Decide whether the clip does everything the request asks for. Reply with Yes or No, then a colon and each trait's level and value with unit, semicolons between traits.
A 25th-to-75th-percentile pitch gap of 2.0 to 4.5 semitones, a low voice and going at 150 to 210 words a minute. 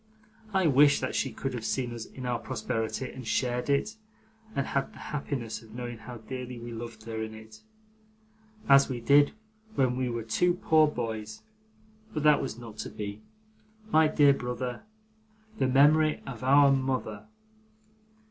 Yes: average, 3.6 semitones; low, 125 Hz; average, 165 wpm